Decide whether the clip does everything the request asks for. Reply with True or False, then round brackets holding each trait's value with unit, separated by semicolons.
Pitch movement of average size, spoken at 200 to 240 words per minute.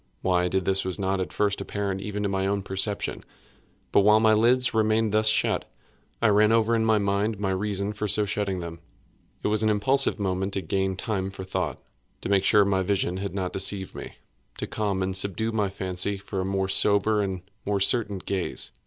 False (1.9 semitones; 205 wpm)